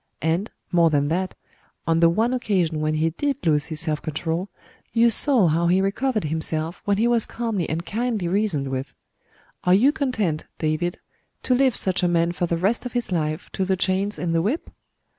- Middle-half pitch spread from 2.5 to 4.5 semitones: No, average, 5.3 semitones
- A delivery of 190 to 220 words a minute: Yes, average, 200 wpm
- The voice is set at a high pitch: No, medium, 180 Hz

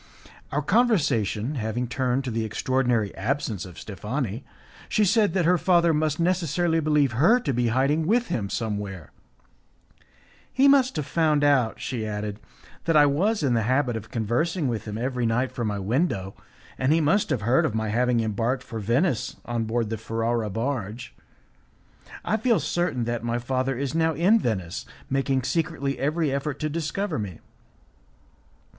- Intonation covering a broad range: Yes, wide, 5.8 semitones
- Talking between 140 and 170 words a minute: Yes, average, 165 wpm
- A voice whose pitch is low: Yes, low, 130 Hz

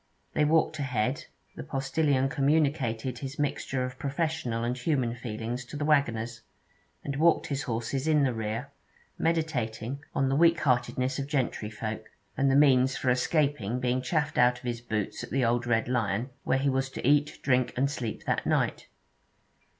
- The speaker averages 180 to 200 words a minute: No, average, 170 wpm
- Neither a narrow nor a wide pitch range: Yes, average, 3.1 semitones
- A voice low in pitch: Yes, low, 130 Hz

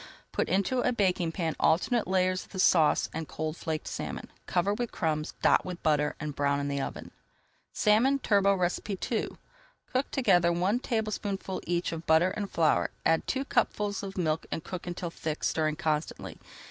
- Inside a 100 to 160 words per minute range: No, average, 170 wpm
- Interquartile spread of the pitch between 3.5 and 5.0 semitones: Yes, average, 4.2 semitones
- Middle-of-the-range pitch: Yes, medium, 180 Hz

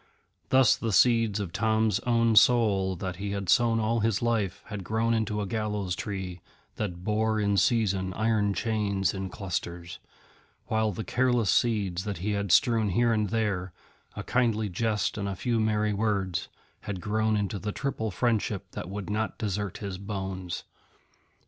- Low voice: Yes, low, 105 Hz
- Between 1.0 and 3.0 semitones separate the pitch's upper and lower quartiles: Yes, narrow, 2.5 semitones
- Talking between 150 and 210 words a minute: Yes, average, 165 wpm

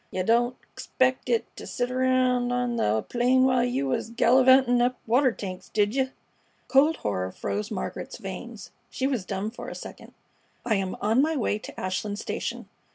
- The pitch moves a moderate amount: Yes, average, 3.7 semitones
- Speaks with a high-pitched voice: Yes, high, 245 Hz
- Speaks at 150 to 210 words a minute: Yes, average, 175 wpm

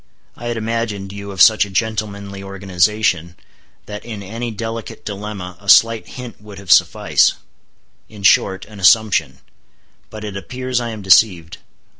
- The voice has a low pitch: Yes, low, 105 Hz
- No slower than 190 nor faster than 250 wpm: No, average, 145 wpm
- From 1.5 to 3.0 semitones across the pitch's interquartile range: Yes, narrow, 2.4 semitones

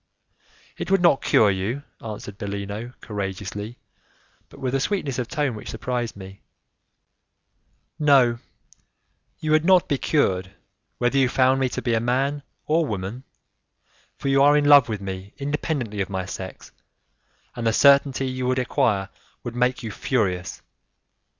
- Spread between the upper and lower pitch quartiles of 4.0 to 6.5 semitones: Yes, average, 5.3 semitones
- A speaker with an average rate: Yes, average, 150 wpm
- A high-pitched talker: No, low, 125 Hz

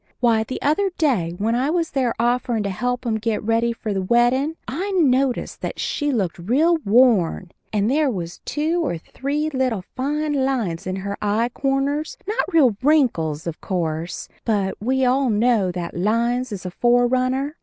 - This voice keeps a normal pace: Yes, average, 175 wpm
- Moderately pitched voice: No, high, 240 Hz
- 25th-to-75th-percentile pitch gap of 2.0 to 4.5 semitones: No, average, 5.2 semitones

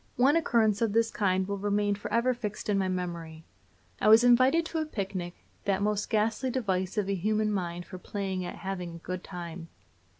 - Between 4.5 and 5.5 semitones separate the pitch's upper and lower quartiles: No, average, 3.4 semitones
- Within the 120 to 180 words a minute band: No, average, 195 wpm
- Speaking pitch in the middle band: No, high, 200 Hz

